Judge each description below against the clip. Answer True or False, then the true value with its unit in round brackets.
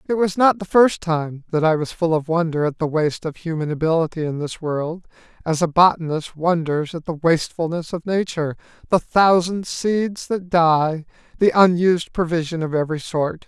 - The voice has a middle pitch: True (165 Hz)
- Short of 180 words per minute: False (185 wpm)